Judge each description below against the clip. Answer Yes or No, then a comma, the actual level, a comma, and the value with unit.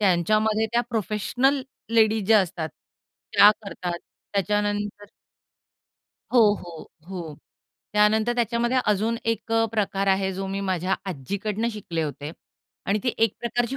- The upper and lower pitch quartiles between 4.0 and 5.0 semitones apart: No, average, 2.9 semitones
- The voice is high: Yes, high, 210 Hz